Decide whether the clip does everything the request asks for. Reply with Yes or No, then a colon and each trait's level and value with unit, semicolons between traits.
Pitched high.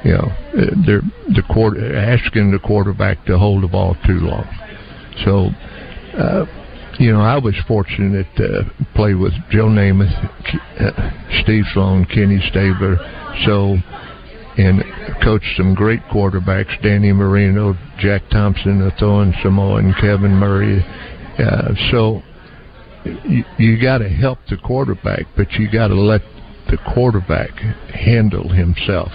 No: low, 100 Hz